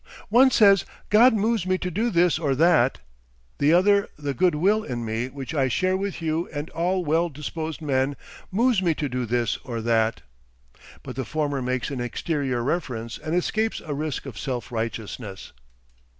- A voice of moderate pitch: Yes, medium, 150 Hz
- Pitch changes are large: Yes, wide, 6.2 semitones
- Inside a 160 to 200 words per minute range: Yes, average, 180 wpm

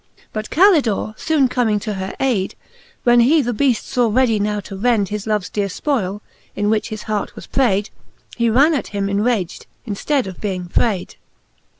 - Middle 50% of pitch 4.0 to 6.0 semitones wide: No, average, 3.5 semitones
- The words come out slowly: No, average, 185 wpm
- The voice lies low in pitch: No, high, 215 Hz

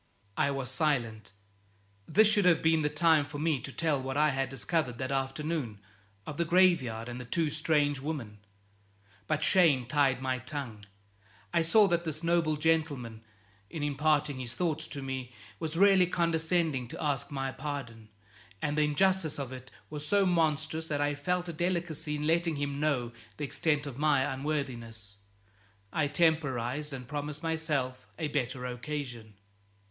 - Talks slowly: No, average, 165 wpm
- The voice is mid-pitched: Yes, medium, 145 Hz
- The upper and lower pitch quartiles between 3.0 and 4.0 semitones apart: Yes, average, 3.6 semitones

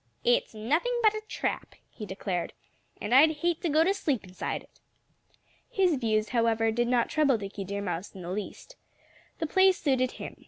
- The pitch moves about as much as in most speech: No, wide, 7.3 semitones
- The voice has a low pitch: No, high, 245 Hz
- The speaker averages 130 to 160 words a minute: No, average, 185 wpm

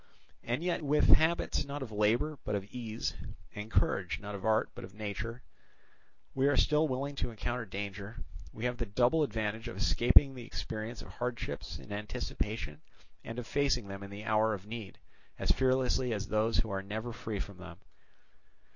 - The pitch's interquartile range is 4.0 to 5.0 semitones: No, average, 3.3 semitones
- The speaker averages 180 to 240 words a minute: Yes, average, 185 wpm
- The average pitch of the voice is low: Yes, low, 115 Hz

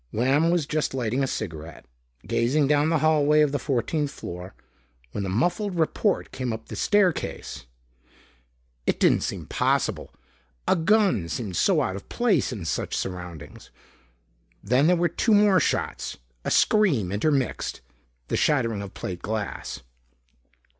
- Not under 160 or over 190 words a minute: No, average, 145 wpm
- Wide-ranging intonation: Yes, wide, 7.9 semitones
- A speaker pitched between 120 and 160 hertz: Yes, low, 135 Hz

